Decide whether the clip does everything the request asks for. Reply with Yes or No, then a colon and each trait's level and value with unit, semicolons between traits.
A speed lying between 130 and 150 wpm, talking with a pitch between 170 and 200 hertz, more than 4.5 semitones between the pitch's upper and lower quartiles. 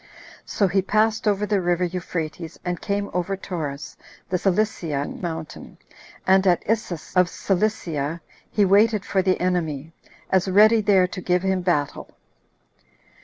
No: average, 140 wpm; medium, 185 Hz; average, 2.7 semitones